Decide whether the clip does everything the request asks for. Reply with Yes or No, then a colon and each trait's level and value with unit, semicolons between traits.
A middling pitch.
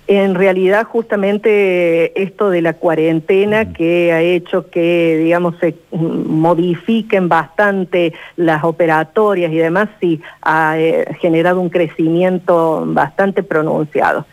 Yes: medium, 175 Hz